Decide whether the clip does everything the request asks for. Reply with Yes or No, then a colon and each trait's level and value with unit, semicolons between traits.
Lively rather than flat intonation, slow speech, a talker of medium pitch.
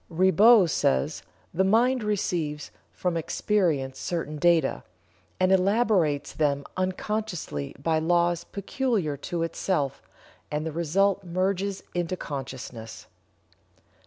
No: average, 4.6 semitones; slow, 100 wpm; medium, 175 Hz